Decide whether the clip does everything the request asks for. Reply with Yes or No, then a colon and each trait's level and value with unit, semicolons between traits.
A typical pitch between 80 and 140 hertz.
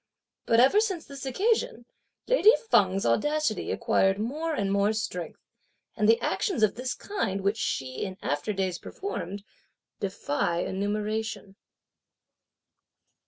No: high, 215 Hz